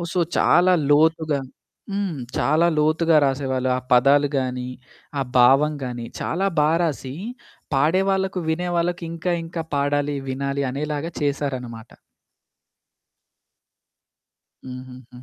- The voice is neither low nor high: Yes, medium, 145 Hz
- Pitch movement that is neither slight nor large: Yes, average, 4.2 semitones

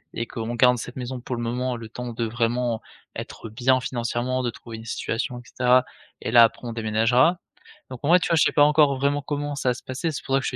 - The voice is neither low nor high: No, low, 125 Hz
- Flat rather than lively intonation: Yes, narrow, 2.1 semitones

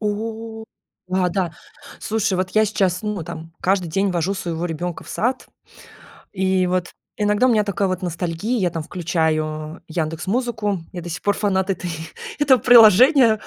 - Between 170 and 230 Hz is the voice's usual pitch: Yes, high, 190 Hz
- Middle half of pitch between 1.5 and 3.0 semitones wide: No, average, 3.8 semitones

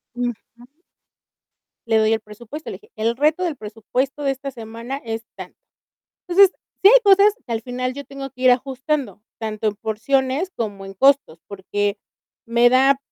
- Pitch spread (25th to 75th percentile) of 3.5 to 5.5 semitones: Yes, average, 4.0 semitones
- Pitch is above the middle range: Yes, very high, 250 Hz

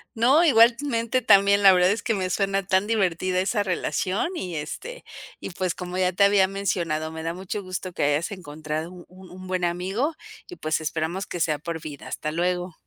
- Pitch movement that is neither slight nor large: Yes, average, 3.0 semitones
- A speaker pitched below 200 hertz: Yes, medium, 185 Hz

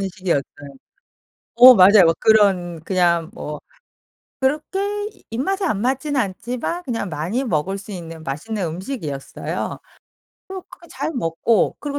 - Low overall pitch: No, high, 200 Hz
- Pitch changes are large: Yes, wide, 7.2 semitones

